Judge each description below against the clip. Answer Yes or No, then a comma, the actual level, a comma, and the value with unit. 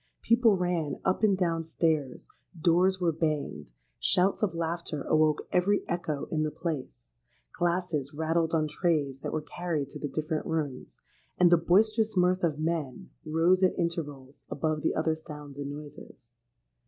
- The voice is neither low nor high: Yes, medium, 160 Hz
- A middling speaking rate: Yes, average, 155 wpm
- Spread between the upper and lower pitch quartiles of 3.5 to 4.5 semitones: No, average, 2.9 semitones